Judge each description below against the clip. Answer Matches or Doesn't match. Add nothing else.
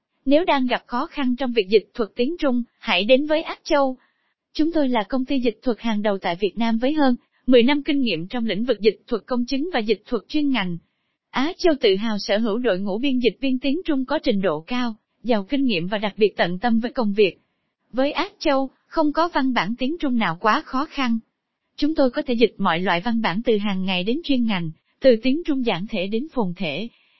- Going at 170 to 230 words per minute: Doesn't match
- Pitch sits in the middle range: Doesn't match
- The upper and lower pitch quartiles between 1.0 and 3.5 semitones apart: Doesn't match